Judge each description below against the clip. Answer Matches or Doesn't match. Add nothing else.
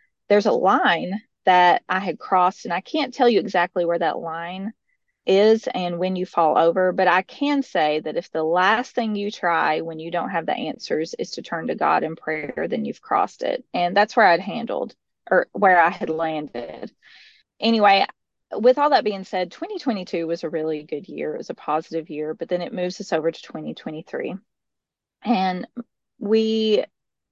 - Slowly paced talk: Doesn't match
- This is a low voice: Doesn't match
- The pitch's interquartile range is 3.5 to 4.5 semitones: Doesn't match